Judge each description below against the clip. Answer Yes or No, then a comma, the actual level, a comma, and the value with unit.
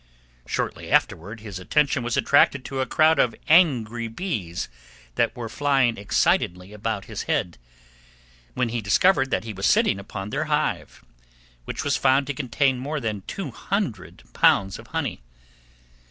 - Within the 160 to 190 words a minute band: No, average, 150 wpm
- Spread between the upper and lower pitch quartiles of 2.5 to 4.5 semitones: No, average, 5.3 semitones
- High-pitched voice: No, low, 120 Hz